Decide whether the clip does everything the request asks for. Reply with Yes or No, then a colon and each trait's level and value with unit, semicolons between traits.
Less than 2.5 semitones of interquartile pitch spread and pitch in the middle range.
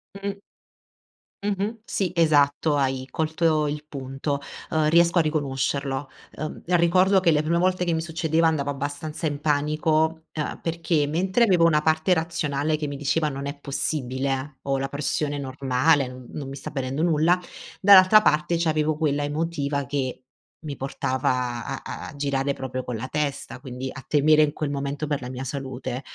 No: average, 2.8 semitones; medium, 150 Hz